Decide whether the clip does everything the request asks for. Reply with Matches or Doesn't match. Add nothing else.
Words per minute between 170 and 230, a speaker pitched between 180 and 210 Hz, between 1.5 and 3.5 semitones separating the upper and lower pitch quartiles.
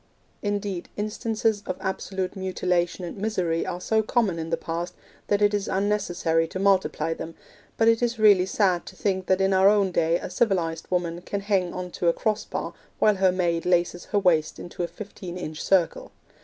Matches